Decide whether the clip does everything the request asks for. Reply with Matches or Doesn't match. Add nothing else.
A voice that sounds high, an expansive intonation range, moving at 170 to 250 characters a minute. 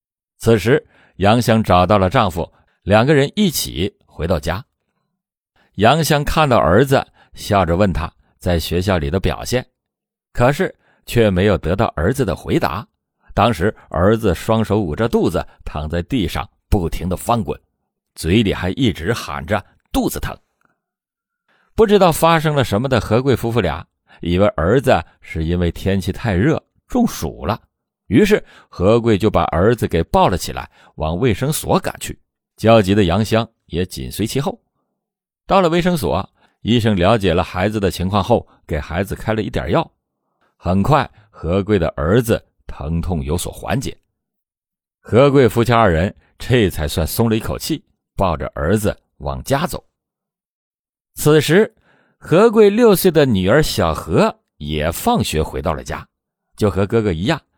Doesn't match